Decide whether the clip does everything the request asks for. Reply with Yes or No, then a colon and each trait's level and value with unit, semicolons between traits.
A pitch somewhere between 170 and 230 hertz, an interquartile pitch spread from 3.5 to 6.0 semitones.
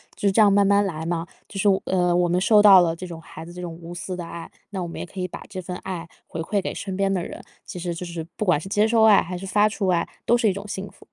No: medium, 185 Hz; average, 2.7 semitones